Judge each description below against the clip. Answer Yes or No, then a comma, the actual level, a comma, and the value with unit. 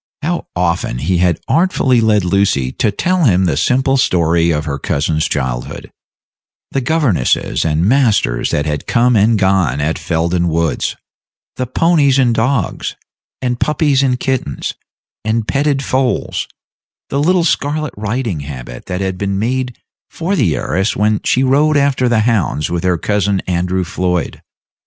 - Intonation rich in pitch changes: Yes, wide, 7.6 semitones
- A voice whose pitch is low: Yes, low, 105 Hz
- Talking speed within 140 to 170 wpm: Yes, average, 150 wpm